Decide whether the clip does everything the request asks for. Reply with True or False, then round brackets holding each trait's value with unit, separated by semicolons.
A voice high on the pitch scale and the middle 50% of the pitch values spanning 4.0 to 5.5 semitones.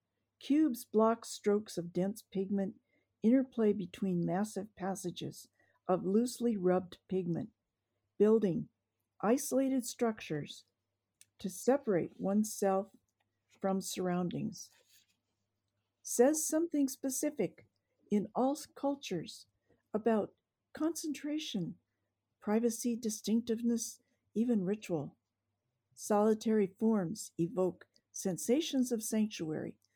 True (210 Hz; 5.2 semitones)